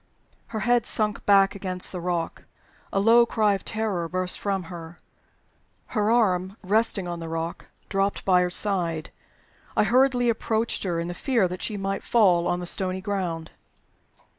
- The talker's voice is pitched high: Yes, high, 195 Hz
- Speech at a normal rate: Yes, average, 165 wpm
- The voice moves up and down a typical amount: Yes, average, 3.4 semitones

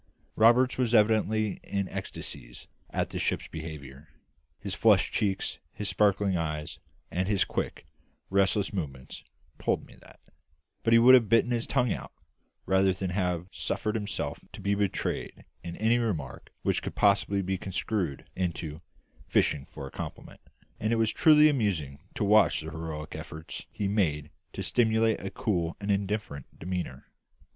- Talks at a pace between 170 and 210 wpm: No, average, 155 wpm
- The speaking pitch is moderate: No, low, 100 Hz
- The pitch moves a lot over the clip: No, average, 4.9 semitones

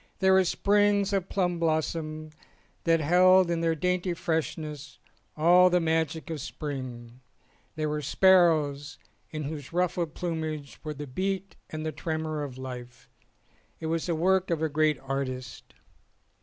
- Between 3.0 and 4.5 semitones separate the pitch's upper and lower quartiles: Yes, average, 3.3 semitones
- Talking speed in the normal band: Yes, average, 150 wpm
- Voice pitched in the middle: Yes, medium, 160 Hz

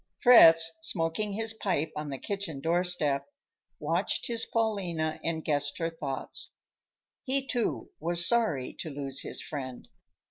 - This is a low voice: No, medium, 165 Hz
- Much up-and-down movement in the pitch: Yes, wide, 5.8 semitones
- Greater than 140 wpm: No, slow, 135 wpm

